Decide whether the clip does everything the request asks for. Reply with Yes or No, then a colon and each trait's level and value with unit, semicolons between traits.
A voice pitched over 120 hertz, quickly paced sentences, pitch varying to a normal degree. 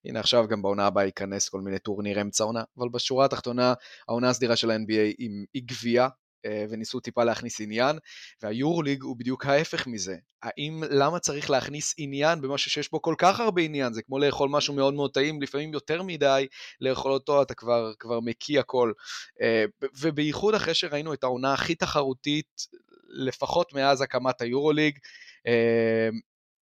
Yes: low, 135 Hz; fast, 165 wpm; average, 4.1 semitones